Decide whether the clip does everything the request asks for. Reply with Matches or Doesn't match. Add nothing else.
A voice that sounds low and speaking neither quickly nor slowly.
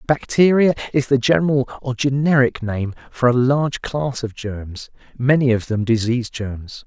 Matches